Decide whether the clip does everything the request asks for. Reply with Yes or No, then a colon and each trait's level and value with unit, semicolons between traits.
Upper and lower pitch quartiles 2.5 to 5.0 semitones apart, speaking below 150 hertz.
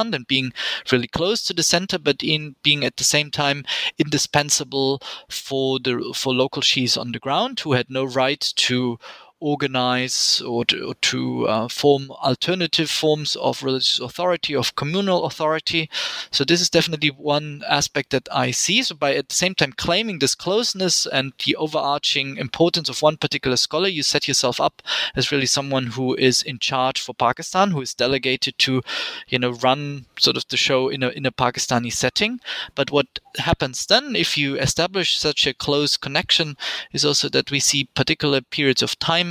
Yes: average, 3.2 semitones; medium, 140 Hz